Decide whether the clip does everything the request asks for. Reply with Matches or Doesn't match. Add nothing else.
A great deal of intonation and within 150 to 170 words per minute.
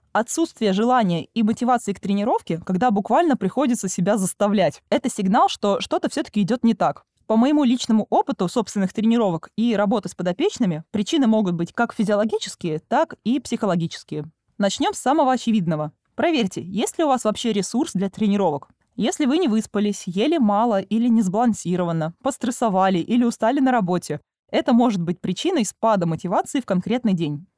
Doesn't match